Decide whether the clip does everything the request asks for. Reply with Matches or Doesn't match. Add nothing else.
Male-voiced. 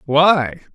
Matches